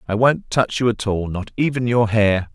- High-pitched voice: No, low, 110 Hz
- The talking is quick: Yes, fast, 210 wpm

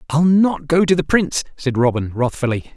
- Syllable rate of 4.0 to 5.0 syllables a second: No, 5.4 syllables/s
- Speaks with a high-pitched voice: No, medium, 150 Hz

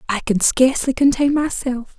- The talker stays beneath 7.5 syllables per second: Yes, 5.0 syllables/s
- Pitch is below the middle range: No, very high, 260 Hz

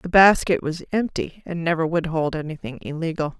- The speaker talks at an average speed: Yes, average, 175 wpm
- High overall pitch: No, medium, 165 Hz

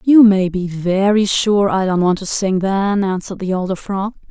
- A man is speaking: No, female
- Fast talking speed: Yes, fast, 210 wpm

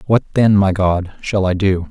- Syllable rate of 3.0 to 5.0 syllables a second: Yes, 4.4 syllables/s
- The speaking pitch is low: Yes, low, 100 Hz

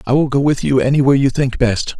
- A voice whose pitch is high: No, low, 135 Hz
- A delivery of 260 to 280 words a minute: Yes, fast, 270 wpm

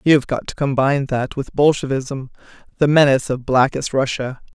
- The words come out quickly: No, average, 155 wpm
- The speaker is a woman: Yes, female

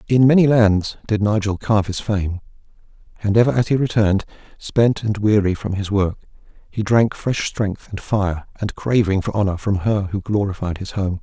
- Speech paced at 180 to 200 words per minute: Yes, average, 185 wpm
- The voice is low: Yes, low, 105 Hz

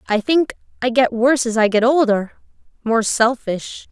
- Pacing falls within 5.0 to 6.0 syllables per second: No, 4.7 syllables/s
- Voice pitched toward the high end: Yes, high, 240 Hz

